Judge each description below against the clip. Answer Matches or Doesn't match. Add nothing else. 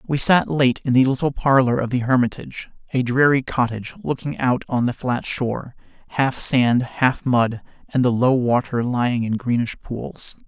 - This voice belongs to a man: Matches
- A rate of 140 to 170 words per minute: Doesn't match